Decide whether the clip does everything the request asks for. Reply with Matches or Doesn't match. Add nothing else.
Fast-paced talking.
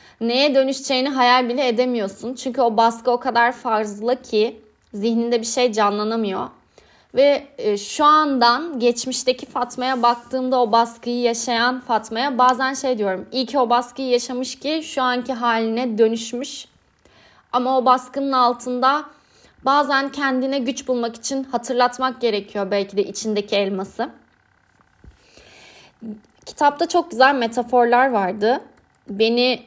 Doesn't match